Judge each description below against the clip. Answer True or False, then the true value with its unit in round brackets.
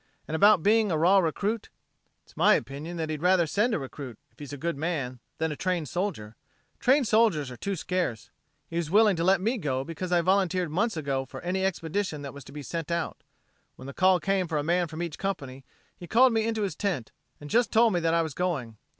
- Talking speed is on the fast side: True (235 wpm)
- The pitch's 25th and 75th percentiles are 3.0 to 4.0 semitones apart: False (4.7 semitones)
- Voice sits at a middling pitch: True (170 Hz)